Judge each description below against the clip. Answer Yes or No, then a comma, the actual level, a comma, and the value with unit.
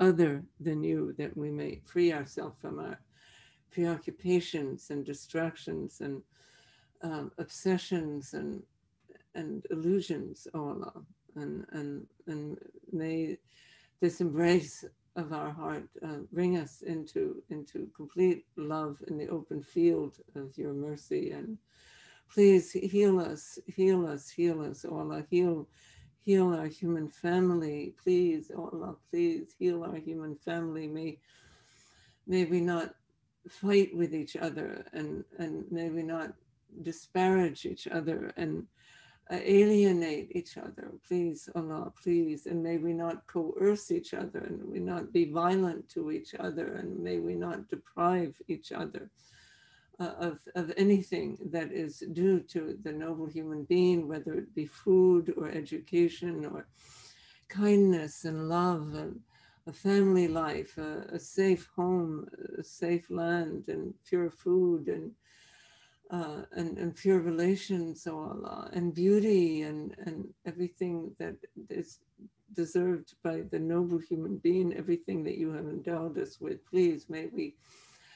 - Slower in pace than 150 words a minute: Yes, average, 140 wpm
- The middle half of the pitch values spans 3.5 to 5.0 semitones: No, narrow, 2.6 semitones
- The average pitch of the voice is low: No, medium, 170 Hz